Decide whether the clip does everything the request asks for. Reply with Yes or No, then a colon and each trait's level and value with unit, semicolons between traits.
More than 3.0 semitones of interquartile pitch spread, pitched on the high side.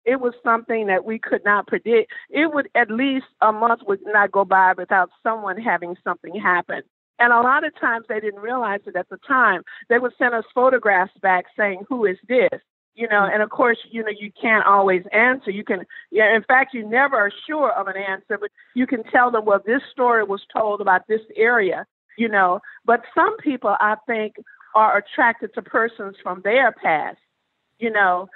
Yes: average, 3.7 semitones; high, 220 Hz